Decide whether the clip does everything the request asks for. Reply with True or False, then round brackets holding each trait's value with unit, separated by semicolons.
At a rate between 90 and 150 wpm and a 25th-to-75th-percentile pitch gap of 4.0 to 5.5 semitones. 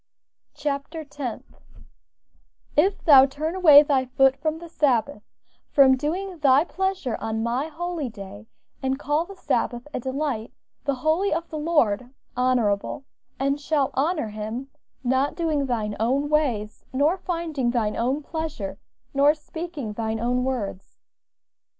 True (140 wpm; 4.4 semitones)